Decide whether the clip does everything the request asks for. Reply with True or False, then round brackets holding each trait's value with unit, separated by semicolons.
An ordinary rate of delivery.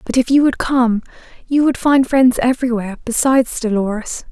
True (165 wpm)